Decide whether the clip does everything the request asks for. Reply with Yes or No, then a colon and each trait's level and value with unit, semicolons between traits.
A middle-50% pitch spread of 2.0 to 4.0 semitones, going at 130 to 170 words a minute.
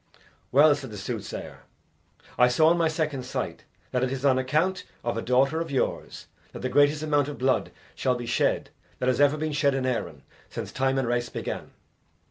No: average, 2.9 semitones; average, 200 wpm